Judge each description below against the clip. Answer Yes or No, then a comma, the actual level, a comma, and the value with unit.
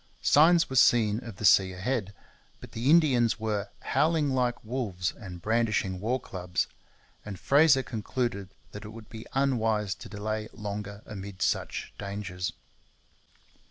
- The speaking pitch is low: Yes, low, 110 Hz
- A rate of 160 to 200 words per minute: No, average, 140 wpm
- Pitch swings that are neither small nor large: Yes, average, 3.7 semitones